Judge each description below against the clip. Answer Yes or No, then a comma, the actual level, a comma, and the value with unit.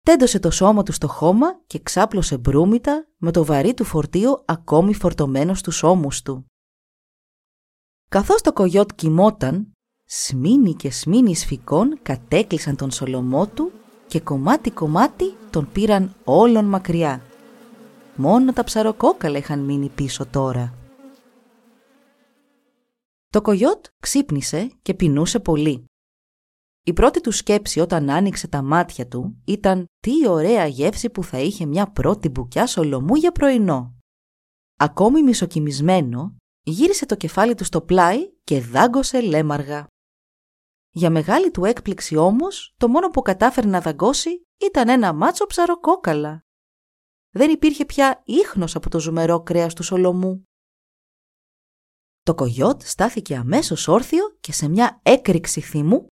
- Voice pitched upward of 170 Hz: Yes, high, 190 Hz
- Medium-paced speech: Yes, average, 125 wpm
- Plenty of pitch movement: Yes, wide, 8.2 semitones